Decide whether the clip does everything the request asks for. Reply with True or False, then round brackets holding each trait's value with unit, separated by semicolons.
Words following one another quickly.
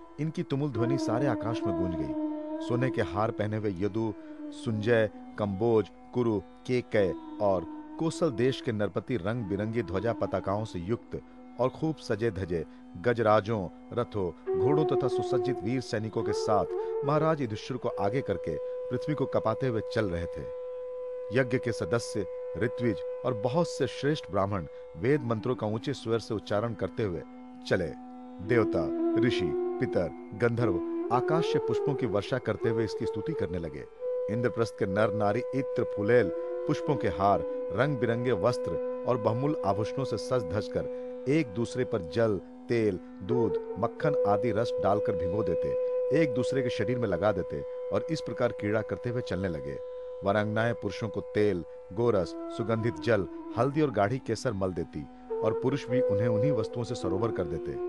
False (160 wpm)